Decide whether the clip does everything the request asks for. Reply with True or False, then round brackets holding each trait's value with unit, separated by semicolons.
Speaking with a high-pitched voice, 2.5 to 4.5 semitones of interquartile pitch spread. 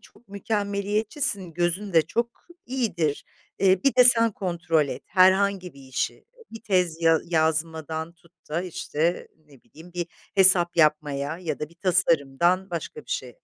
False (175 Hz; 3.8 semitones)